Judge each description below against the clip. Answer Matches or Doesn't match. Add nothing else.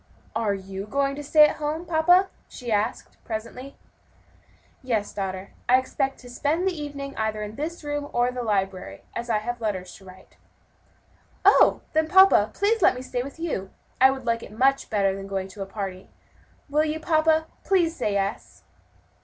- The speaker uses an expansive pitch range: Matches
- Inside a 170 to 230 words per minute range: Matches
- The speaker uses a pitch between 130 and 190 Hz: Doesn't match